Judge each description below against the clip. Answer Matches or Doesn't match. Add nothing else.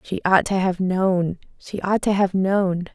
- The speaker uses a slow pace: Doesn't match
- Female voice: Matches